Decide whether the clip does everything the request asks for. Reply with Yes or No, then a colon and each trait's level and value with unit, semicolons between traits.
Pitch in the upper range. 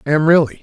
No: medium, 155 Hz